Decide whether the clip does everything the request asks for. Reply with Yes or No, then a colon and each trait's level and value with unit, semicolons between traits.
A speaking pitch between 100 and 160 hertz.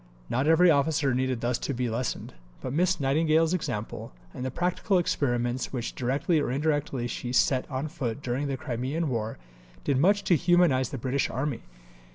Yes: low, 135 Hz